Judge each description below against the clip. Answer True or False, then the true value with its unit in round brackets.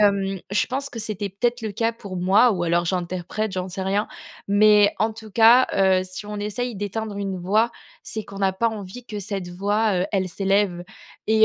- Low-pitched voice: False (205 Hz)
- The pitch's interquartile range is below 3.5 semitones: True (2.5 semitones)